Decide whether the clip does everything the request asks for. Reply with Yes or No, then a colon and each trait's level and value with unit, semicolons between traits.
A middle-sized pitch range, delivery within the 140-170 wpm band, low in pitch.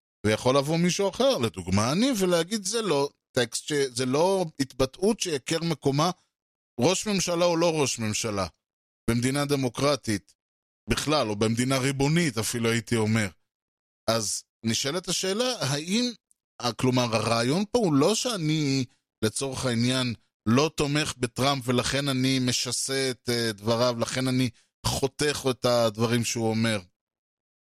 No: average, 5.0 semitones; average, 120 wpm; low, 130 Hz